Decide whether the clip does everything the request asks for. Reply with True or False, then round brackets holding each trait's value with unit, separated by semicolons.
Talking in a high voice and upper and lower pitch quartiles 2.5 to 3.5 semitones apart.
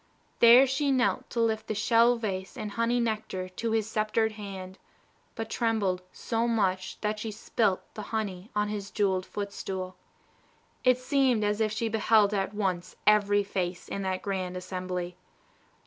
True (210 Hz; 3.0 semitones)